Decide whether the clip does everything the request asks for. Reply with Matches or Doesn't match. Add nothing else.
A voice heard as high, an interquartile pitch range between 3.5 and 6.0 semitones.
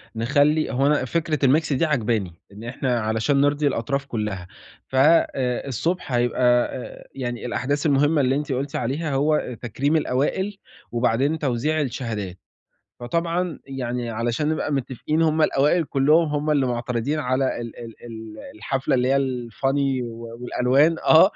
Doesn't match